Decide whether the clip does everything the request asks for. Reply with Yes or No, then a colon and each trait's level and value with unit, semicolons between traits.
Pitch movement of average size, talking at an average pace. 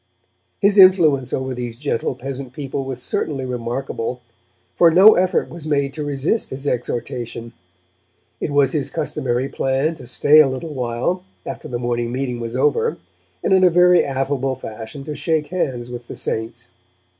Yes: average, 3.8 semitones; average, 165 wpm